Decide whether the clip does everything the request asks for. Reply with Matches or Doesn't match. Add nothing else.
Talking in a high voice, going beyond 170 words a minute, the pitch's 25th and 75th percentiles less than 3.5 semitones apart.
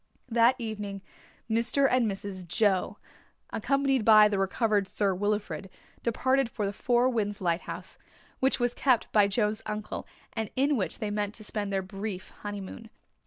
Doesn't match